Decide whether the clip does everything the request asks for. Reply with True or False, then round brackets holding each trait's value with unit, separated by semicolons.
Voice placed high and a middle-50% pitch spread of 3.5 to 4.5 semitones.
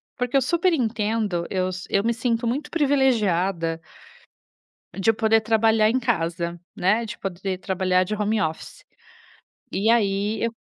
True (215 Hz; 3.8 semitones)